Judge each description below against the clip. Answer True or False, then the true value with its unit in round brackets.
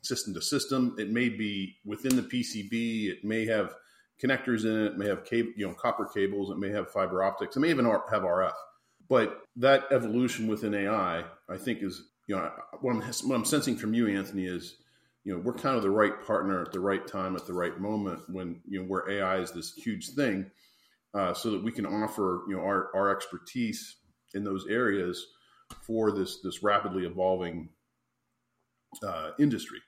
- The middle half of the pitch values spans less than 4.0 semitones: True (3.0 semitones)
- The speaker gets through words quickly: False (195 wpm)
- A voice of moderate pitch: False (105 Hz)